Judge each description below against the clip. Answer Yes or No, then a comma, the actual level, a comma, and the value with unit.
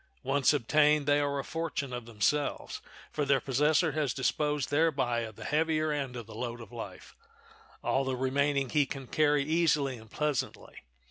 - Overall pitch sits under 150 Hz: Yes, medium, 140 Hz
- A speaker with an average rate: Yes, average, 175 wpm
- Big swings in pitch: No, average, 2.7 semitones